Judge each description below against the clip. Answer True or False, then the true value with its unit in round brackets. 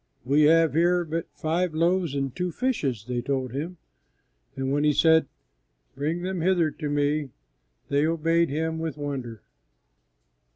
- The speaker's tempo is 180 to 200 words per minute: False (150 wpm)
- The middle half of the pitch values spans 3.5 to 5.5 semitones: False (3.0 semitones)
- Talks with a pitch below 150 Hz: False (155 Hz)